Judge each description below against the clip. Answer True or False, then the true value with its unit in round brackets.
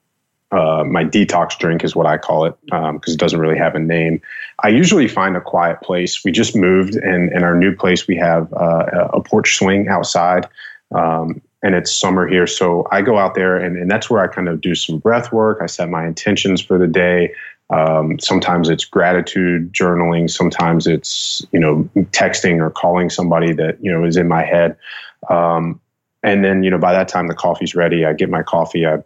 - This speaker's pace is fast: True (210 wpm)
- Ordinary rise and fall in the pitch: False (1.8 semitones)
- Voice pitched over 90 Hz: False (85 Hz)